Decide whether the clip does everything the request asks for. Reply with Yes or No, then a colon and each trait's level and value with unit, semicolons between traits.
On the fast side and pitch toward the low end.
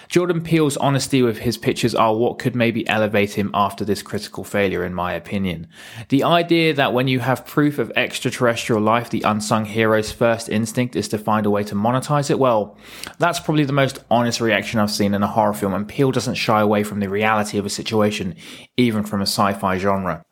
Yes: fast, 210 wpm; low, 110 Hz